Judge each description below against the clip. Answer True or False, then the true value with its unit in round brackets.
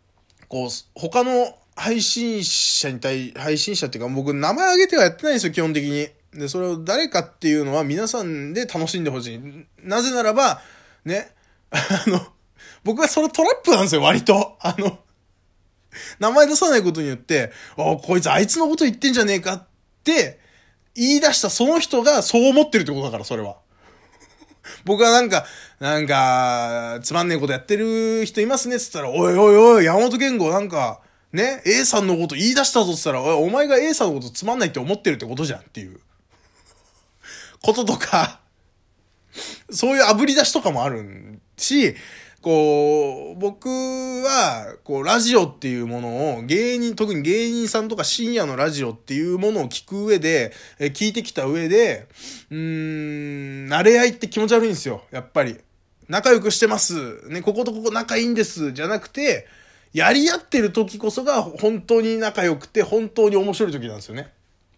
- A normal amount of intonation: False (8.5 semitones)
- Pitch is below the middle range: False (195 Hz)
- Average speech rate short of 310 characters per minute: False (355 characters per minute)